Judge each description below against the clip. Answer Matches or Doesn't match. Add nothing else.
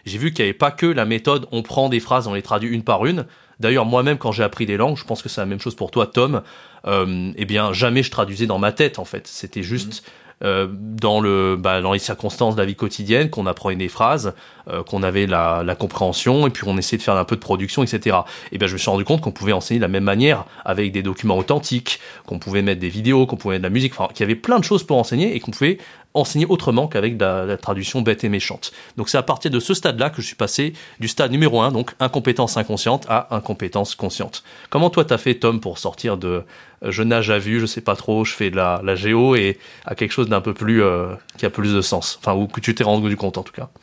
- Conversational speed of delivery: Doesn't match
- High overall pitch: Doesn't match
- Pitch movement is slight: Doesn't match